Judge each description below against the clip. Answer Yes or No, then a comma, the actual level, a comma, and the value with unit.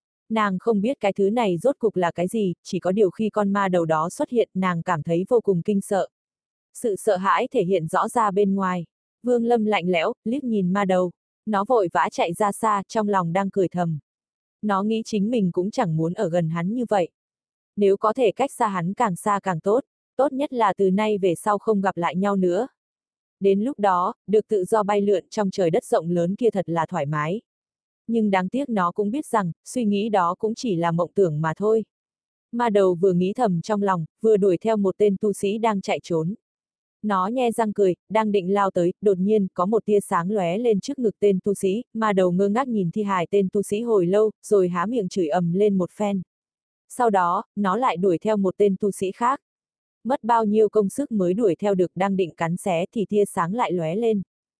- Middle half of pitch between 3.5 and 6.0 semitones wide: No, average, 3.0 semitones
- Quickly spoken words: No, average, 235 wpm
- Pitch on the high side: Yes, high, 200 Hz